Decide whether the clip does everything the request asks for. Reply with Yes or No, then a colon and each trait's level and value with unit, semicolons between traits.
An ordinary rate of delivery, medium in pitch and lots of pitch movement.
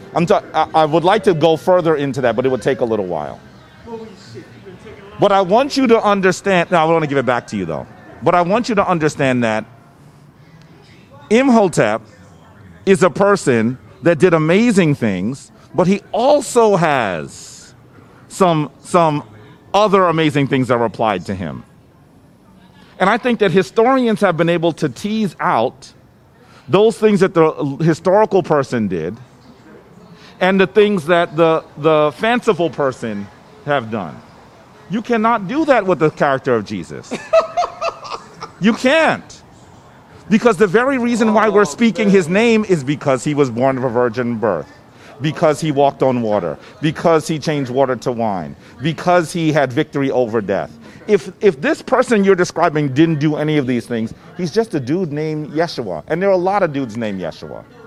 Yes: average, 170 wpm; medium, 165 Hz; wide, 6.4 semitones